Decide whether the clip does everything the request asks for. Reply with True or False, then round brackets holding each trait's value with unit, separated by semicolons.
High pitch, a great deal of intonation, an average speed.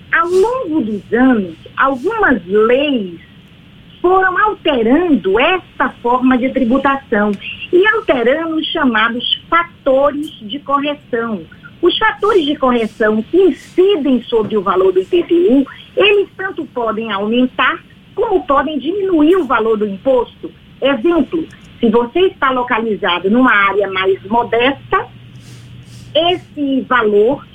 False (275 Hz; 7.2 semitones; 115 wpm)